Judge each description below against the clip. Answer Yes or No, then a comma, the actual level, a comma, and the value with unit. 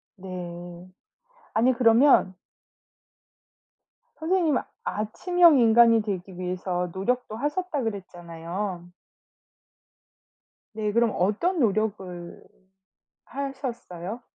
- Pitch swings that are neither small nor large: No, wide, 5.7 semitones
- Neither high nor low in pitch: No, high, 215 Hz